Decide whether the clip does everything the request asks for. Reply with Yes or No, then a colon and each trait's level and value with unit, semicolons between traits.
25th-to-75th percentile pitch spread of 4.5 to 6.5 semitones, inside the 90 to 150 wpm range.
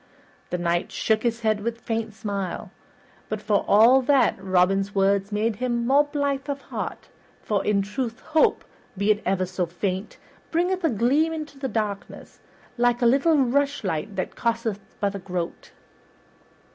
No: average, 5.1 semitones; average, 160 wpm